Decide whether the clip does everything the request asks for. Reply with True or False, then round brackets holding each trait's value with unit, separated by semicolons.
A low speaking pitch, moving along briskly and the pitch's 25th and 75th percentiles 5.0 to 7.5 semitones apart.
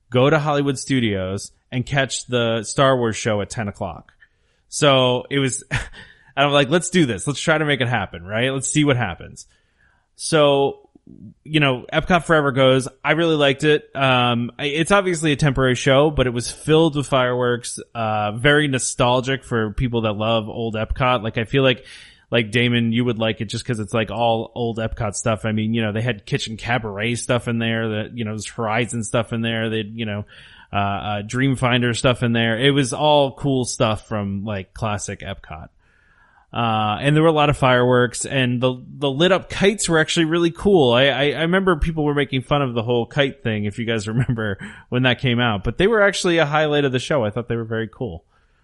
False (125 Hz; 215 wpm; 4.0 semitones)